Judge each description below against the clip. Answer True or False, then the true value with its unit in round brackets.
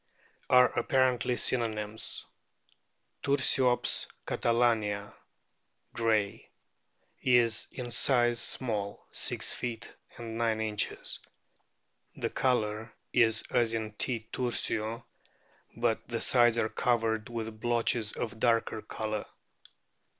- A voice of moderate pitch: False (115 Hz)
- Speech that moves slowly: True (90 wpm)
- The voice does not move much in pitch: True (1.7 semitones)